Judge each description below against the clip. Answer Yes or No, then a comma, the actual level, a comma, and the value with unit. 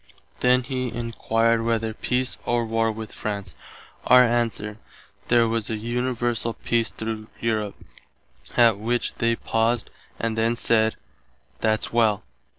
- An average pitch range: No, narrow, 1.3 semitones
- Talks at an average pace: No, slow, 130 wpm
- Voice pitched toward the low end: Yes, low, 115 Hz